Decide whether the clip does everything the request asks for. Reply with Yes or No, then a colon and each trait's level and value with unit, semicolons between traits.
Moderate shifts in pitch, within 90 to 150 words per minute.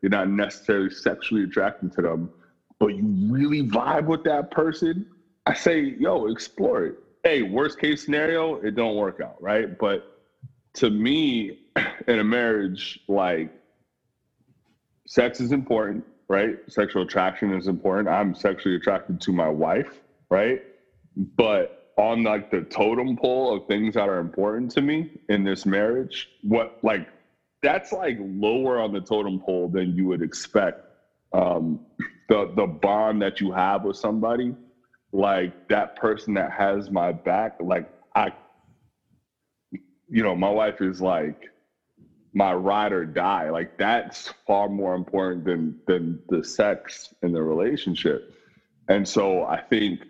No: wide, 6.4 semitones; average, 145 wpm